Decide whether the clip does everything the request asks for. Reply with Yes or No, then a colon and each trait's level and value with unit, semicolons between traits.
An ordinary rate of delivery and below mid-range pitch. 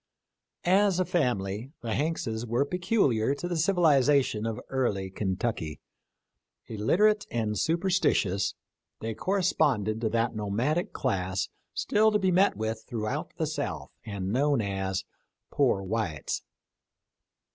No: slow, 130 wpm; low, 120 Hz